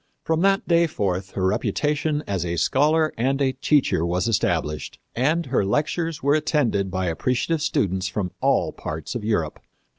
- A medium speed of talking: Yes, average, 160 wpm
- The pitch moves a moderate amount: No, wide, 8.3 semitones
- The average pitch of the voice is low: Yes, low, 125 Hz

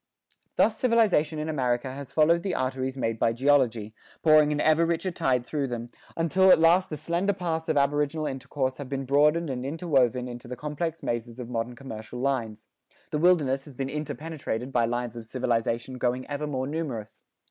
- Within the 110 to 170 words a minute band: No, average, 180 wpm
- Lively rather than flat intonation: No, average, 4.2 semitones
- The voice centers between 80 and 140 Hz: Yes, low, 135 Hz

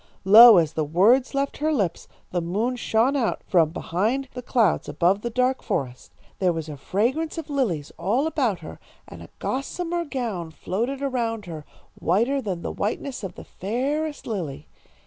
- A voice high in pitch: Yes, high, 225 Hz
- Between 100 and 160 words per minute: No, average, 170 wpm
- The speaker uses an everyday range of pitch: No, wide, 7.3 semitones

